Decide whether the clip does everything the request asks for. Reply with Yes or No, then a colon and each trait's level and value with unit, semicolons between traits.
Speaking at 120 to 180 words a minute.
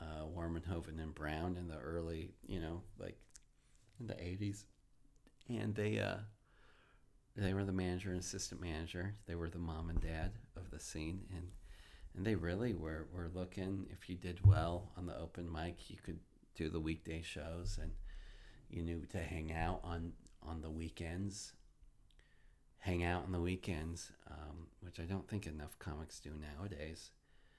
Yes: average, 170 wpm